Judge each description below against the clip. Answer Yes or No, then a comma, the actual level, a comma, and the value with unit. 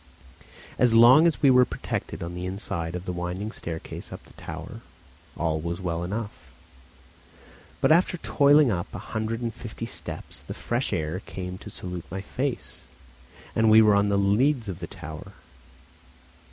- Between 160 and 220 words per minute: Yes, average, 165 wpm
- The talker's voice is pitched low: Yes, low, 100 Hz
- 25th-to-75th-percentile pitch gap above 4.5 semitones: Yes, average, 5.1 semitones